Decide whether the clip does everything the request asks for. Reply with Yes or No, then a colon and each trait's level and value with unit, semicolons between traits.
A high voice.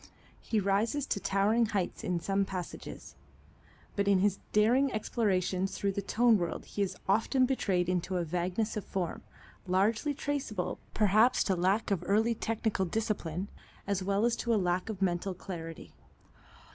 Yes: high, 200 Hz